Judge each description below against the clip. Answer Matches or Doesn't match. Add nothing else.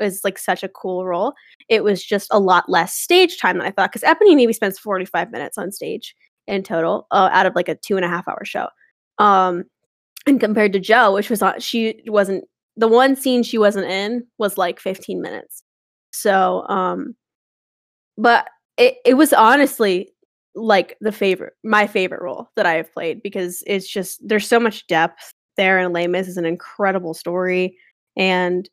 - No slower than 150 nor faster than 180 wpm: Doesn't match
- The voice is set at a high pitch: Matches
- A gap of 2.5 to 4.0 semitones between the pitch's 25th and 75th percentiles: Matches